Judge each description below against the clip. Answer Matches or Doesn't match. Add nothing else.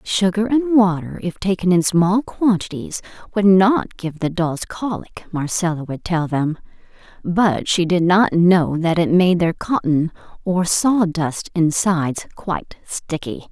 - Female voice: Matches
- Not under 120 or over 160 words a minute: Matches